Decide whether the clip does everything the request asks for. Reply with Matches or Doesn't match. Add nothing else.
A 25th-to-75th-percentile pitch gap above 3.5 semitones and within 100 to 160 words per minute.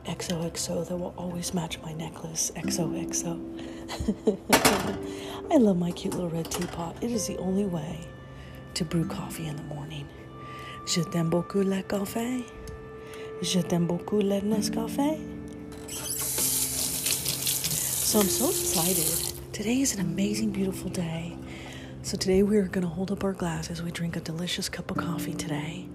Matches